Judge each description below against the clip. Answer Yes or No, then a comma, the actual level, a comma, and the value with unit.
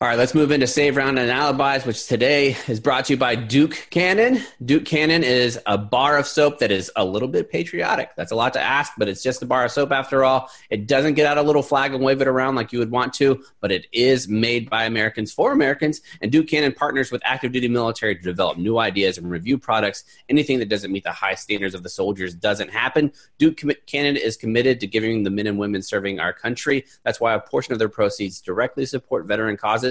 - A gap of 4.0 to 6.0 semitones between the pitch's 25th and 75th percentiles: Yes, average, 4.4 semitones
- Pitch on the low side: Yes, low, 125 Hz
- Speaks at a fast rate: Yes, fast, 245 wpm